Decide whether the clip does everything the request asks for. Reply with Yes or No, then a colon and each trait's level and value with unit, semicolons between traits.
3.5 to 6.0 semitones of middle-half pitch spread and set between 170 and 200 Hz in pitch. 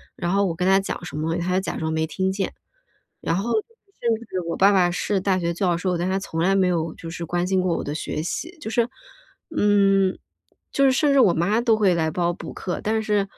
No: average, 3.1 semitones; high, 190 Hz